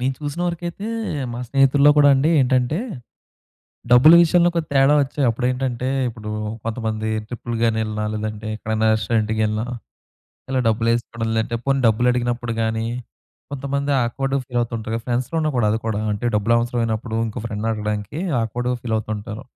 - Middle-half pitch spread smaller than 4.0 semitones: Yes, average, 3.5 semitones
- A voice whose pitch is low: Yes, low, 120 Hz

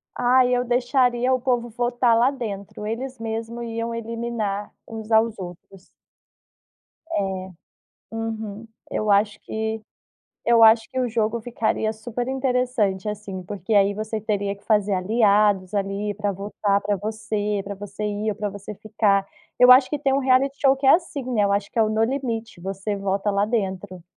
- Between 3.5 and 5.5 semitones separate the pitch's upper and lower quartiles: No, average, 3.0 semitones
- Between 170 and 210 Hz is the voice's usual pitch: No, high, 220 Hz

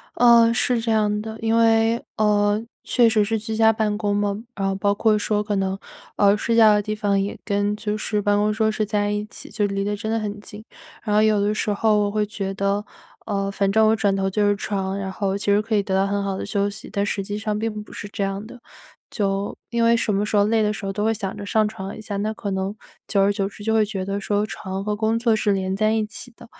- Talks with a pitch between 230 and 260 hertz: No, high, 210 Hz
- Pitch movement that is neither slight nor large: No, narrow, 1.5 semitones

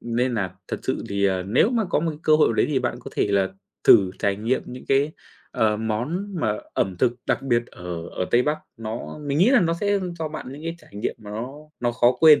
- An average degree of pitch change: No, wide, 6.5 semitones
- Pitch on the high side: No, low, 120 Hz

